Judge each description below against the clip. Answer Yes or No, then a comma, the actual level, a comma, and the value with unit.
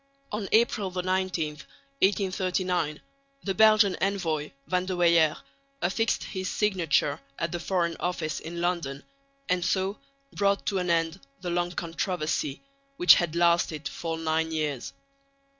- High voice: No, medium, 175 Hz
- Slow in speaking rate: Yes, slow, 130 wpm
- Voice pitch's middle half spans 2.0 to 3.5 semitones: Yes, average, 2.8 semitones